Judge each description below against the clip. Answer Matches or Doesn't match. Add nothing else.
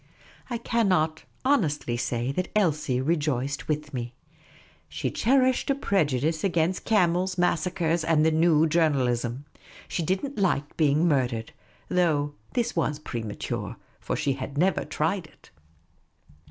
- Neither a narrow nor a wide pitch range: Matches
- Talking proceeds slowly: Matches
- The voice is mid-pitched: Matches